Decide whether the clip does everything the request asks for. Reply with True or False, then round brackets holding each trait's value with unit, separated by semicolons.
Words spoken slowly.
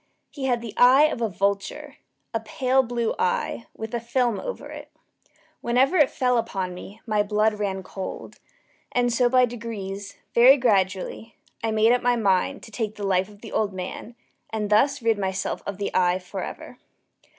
False (180 wpm)